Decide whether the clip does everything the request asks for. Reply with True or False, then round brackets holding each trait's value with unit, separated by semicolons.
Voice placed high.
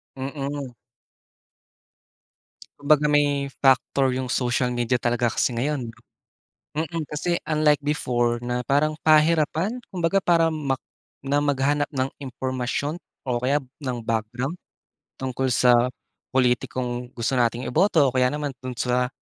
False (135 Hz)